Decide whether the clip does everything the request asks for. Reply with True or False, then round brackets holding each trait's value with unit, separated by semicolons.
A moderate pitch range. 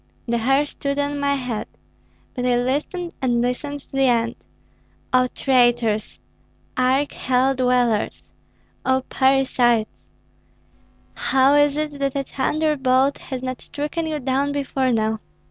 False (2.2 semitones)